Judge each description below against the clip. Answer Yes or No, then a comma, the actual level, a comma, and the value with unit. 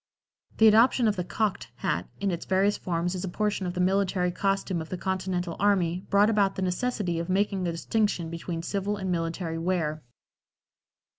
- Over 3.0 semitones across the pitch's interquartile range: No, narrow, 2.6 semitones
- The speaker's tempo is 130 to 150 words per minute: No, average, 180 wpm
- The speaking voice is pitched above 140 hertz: Yes, medium, 185 Hz